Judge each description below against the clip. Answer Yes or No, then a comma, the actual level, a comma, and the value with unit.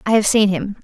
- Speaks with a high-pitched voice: Yes, high, 205 Hz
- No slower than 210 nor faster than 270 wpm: No, fast, 285 wpm